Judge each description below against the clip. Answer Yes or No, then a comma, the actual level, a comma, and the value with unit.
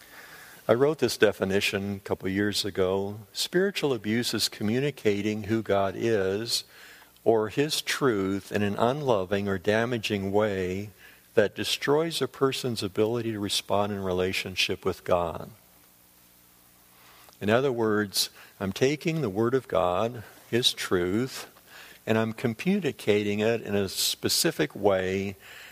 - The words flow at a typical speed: No, slow, 125 wpm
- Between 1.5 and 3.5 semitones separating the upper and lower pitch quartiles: Yes, average, 3.1 semitones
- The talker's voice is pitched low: Yes, low, 105 Hz